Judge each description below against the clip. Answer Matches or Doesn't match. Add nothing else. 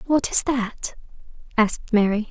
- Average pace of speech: Doesn't match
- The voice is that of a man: Doesn't match